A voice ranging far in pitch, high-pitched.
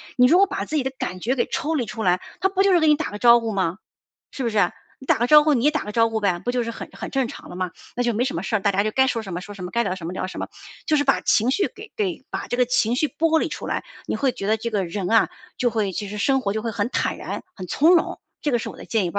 Yes: wide, 5.7 semitones; high, 235 Hz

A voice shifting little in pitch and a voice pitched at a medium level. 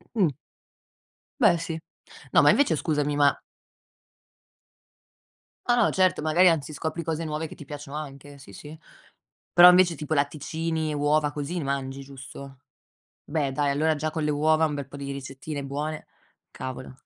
Yes: narrow, 2.3 semitones; medium, 150 Hz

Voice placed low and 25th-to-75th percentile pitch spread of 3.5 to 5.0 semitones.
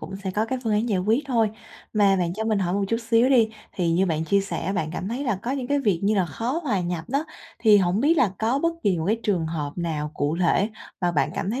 No: high, 200 Hz; average, 4.6 semitones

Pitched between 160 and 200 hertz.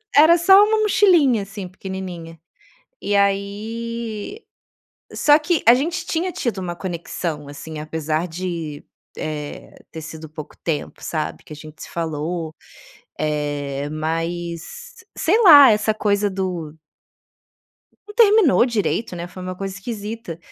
Yes: high, 190 Hz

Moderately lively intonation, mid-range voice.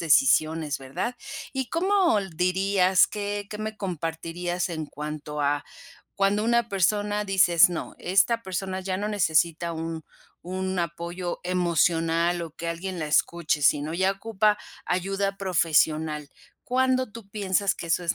Yes: average, 3.6 semitones; medium, 180 Hz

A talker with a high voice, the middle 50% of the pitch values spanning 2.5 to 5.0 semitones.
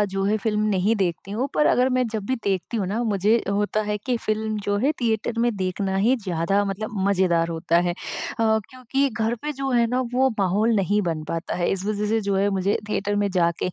Yes: high, 205 Hz; average, 2.9 semitones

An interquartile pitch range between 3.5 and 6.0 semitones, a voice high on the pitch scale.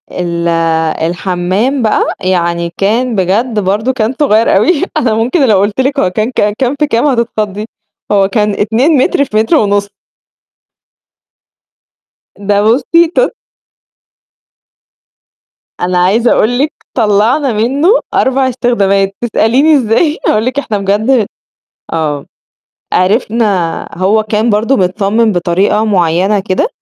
Yes: average, 4.2 semitones; high, 215 Hz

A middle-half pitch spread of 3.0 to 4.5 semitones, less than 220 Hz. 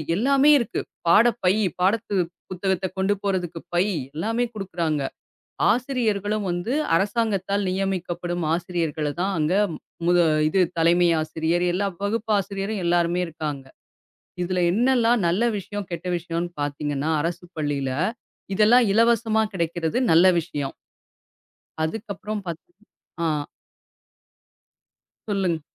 Yes: average, 3.8 semitones; medium, 185 Hz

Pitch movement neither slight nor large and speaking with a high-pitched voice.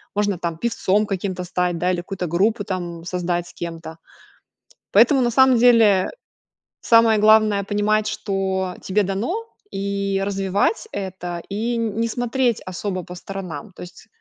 Yes: average, 3.1 semitones; high, 195 Hz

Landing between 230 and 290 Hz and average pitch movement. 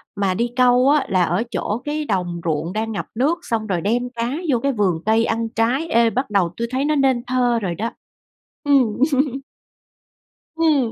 Yes: high, 235 Hz; average, 4.4 semitones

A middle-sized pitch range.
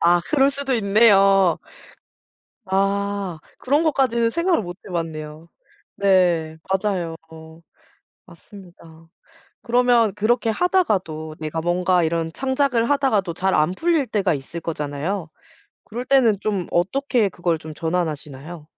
No: wide, 6.0 semitones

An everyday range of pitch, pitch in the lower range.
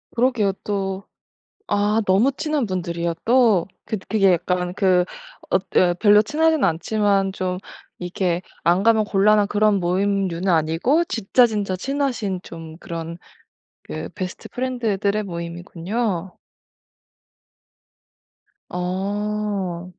No: average, 3.2 semitones; high, 195 Hz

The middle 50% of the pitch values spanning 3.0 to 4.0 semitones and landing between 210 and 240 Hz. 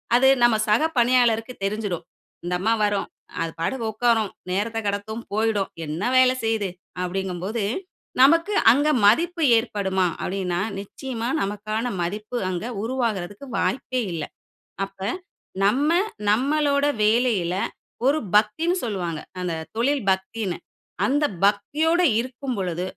No: average, 4.5 semitones; high, 220 Hz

